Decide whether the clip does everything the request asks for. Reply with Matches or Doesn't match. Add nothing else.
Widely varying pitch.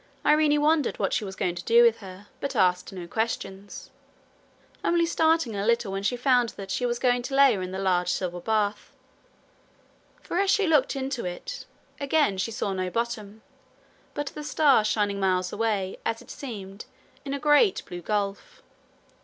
Matches